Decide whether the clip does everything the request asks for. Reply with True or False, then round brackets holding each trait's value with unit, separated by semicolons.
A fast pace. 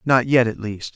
True (250 wpm)